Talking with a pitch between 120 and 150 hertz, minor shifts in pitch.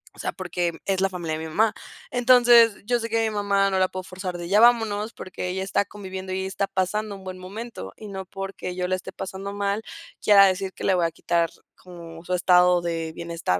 No: high, 190 Hz; narrow, 2.2 semitones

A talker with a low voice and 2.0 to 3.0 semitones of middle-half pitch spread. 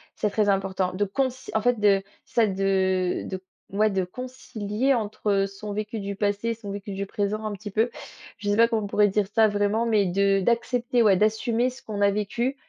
No: high, 210 Hz; narrow, 2.4 semitones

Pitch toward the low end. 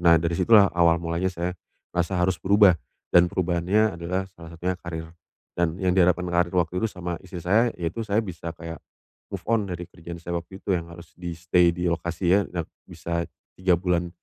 Yes: very low, 90 Hz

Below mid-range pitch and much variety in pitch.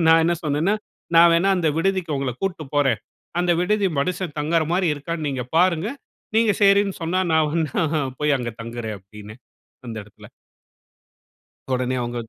No: medium, 160 Hz; wide, 5.8 semitones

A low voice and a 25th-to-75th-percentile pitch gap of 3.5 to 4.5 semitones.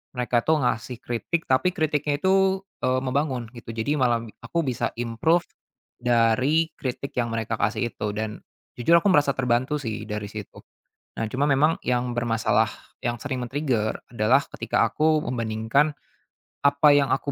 Yes: low, 125 Hz; average, 4.2 semitones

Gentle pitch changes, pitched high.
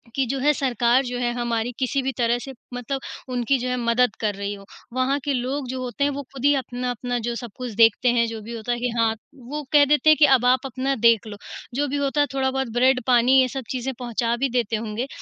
Yes: narrow, 2.2 semitones; very high, 250 Hz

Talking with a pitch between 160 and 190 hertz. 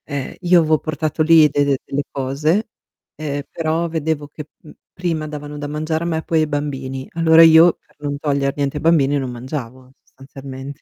No: medium, 150 Hz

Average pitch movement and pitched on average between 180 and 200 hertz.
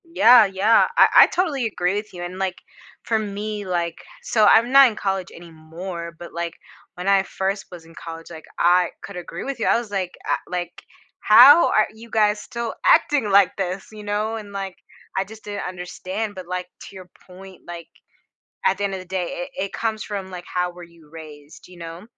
Yes: average, 3.3 semitones; high, 190 Hz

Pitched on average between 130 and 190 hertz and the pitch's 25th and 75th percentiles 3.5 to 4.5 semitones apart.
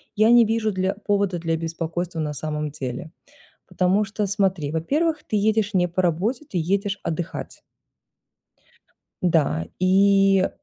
Yes: medium, 185 Hz; average, 3.8 semitones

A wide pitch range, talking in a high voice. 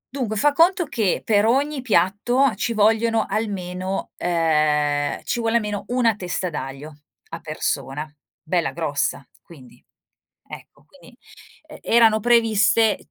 Yes: wide, 5.8 semitones; high, 210 Hz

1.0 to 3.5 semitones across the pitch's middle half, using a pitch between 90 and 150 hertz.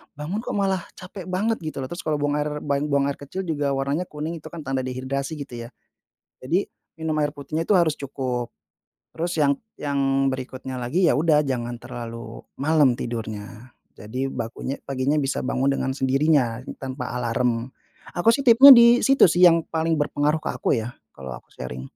No: average, 4.1 semitones; medium, 140 Hz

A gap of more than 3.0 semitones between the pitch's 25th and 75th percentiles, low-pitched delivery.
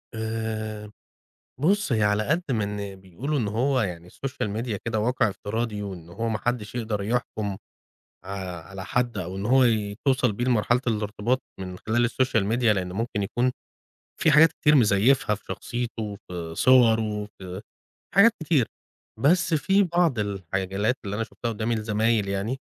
Yes: average, 3.5 semitones; low, 110 Hz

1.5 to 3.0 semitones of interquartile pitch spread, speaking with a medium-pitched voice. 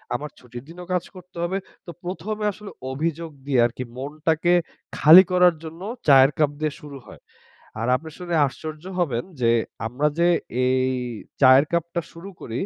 No: average, 4.6 semitones; medium, 155 Hz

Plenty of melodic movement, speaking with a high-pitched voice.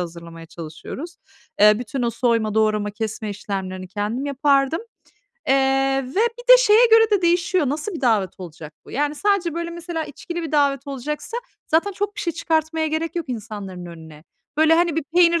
Yes: wide, 8.2 semitones; very high, 280 Hz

